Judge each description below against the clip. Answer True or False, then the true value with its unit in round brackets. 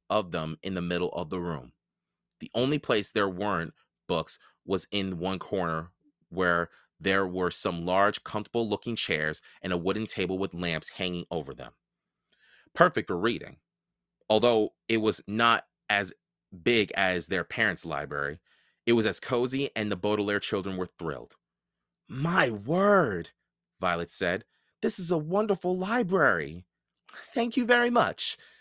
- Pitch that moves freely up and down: True (7.7 semitones)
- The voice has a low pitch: True (100 Hz)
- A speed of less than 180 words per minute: True (150 wpm)